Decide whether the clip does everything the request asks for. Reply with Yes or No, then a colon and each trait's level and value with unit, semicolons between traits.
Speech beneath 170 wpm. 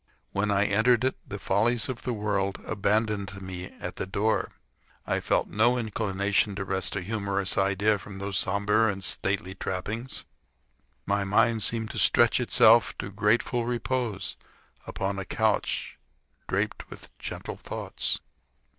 Yes: average, 145 wpm